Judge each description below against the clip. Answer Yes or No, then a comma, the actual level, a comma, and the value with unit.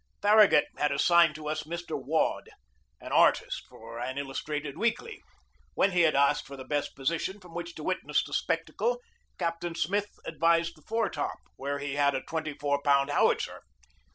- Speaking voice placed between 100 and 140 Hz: No, medium, 155 Hz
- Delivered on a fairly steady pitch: No, average, 3.5 semitones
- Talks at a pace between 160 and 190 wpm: Yes, average, 170 wpm